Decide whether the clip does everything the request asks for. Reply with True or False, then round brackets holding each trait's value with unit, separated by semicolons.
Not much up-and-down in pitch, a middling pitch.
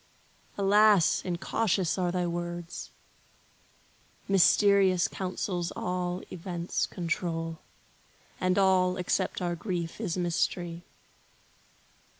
True (1.6 semitones; 180 Hz)